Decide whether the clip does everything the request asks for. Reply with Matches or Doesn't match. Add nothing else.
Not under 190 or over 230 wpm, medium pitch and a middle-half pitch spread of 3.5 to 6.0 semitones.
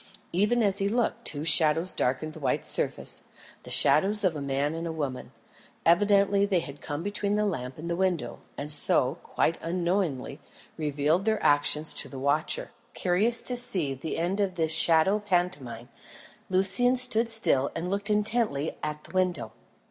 Doesn't match